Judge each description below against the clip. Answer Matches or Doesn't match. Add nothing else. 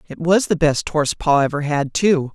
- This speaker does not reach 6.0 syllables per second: Matches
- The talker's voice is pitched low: Doesn't match